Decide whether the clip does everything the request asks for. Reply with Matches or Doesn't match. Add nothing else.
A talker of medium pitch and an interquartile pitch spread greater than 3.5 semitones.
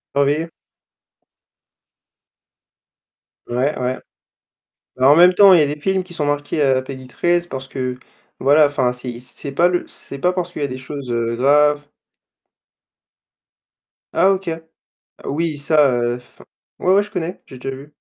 Matches